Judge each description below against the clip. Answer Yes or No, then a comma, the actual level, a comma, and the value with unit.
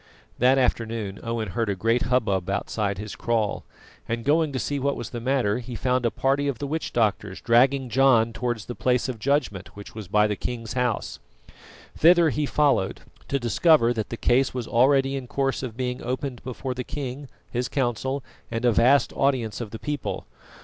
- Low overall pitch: Yes, low, 125 Hz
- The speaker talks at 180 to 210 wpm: Yes, average, 190 wpm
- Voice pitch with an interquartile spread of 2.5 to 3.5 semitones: Yes, average, 3.1 semitones